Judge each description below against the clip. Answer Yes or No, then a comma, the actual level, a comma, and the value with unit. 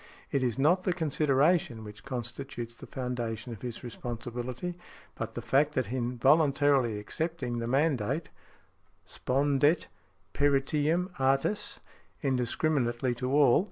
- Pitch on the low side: Yes, low, 130 Hz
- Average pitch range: Yes, average, 3.5 semitones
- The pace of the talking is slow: Yes, slow, 120 wpm